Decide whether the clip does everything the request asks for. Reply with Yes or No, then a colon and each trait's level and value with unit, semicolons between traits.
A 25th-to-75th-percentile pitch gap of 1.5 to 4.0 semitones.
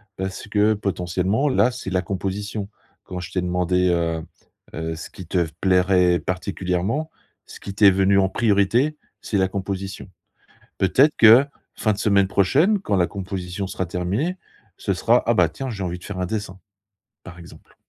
Yes: narrow, 2.4 semitones